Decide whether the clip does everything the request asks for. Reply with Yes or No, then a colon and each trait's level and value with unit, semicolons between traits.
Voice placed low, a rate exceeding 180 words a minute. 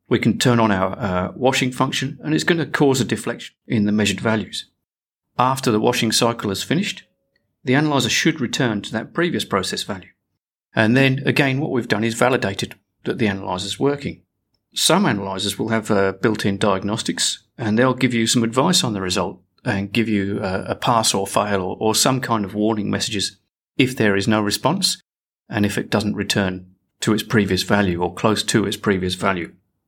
Yes: low, 110 Hz; average, 200 wpm